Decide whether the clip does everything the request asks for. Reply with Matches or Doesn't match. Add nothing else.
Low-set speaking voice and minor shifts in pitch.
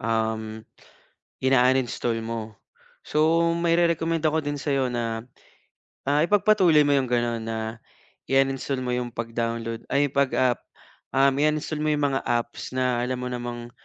Doesn't match